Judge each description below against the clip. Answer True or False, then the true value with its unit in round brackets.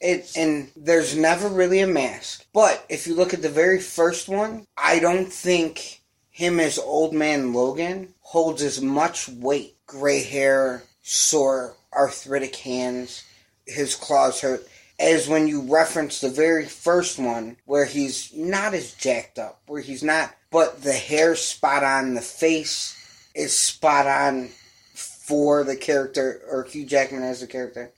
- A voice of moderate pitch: True (145 Hz)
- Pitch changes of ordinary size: True (3.5 semitones)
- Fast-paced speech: False (155 wpm)